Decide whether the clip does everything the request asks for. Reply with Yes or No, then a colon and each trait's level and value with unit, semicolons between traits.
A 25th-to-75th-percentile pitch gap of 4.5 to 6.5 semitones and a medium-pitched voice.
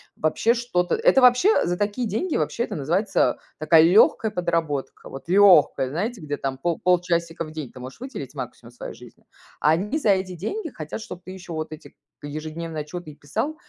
Yes: average, 5.2 semitones; medium, 175 Hz